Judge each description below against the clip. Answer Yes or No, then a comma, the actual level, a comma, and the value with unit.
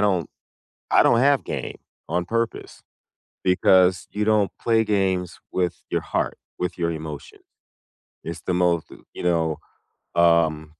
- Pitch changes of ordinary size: Yes, average, 3.5 semitones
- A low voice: Yes, very low, 90 Hz